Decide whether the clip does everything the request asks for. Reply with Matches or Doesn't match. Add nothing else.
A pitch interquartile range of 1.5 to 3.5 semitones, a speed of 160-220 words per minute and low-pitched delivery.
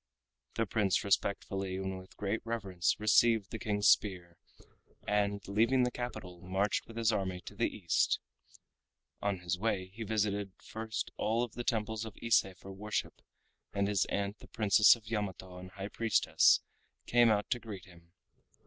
Matches